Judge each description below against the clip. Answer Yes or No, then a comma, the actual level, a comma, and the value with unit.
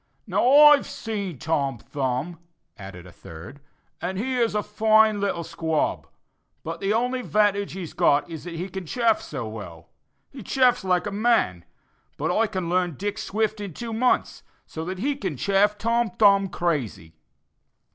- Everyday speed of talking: Yes, average, 165 wpm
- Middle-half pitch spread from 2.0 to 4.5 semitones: No, wide, 5.6 semitones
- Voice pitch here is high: Yes, high, 195 Hz